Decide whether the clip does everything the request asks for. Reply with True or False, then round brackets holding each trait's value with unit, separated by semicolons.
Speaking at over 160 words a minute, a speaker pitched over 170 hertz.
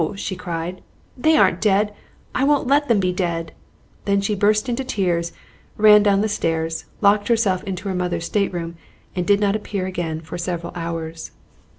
True (175 wpm; 190 Hz)